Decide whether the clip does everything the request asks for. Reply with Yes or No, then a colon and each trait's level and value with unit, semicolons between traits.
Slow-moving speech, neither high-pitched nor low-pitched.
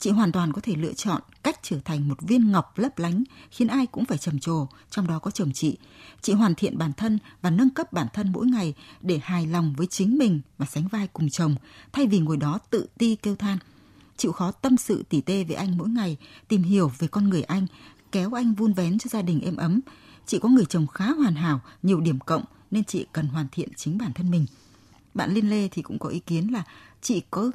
No: average, 245 wpm; medium, 180 Hz